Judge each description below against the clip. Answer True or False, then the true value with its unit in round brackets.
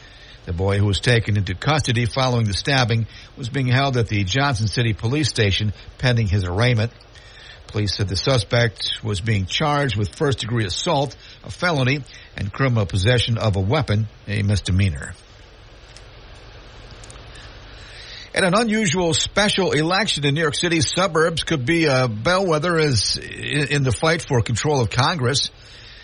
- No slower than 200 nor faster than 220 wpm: False (150 wpm)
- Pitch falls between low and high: False (120 Hz)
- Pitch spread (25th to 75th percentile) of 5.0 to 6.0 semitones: True (5.3 semitones)